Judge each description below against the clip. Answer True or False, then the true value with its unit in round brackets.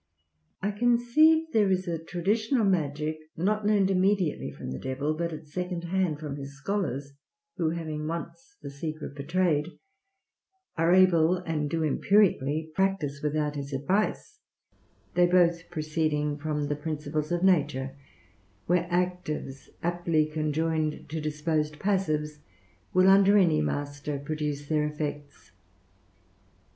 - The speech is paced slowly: True (130 wpm)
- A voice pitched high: False (160 Hz)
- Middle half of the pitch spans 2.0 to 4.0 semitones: True (3.6 semitones)